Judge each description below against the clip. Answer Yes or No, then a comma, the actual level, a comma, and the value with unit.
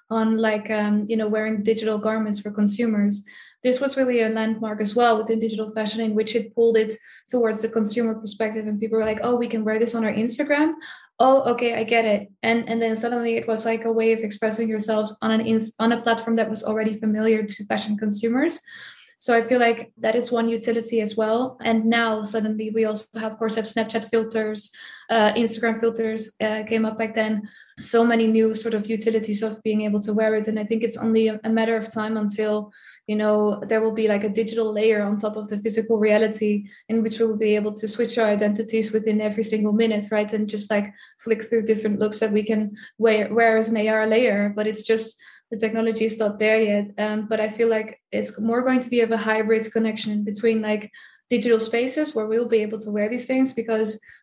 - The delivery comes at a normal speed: No, fast, 225 wpm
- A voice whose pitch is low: No, high, 220 Hz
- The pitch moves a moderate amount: No, narrow, 1.0 semitones